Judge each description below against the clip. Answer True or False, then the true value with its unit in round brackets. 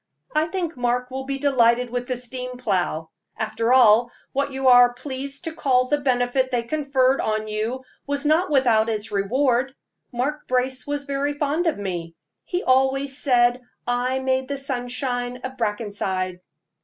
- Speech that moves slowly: False (160 wpm)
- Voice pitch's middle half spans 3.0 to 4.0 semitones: False (2.4 semitones)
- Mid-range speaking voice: False (255 Hz)